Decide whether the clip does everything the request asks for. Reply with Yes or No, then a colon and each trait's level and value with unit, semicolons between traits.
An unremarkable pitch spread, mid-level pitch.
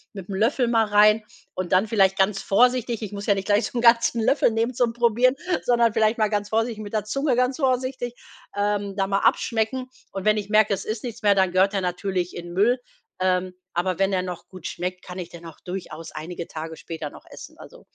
No: average, 3.8 semitones; high, 205 Hz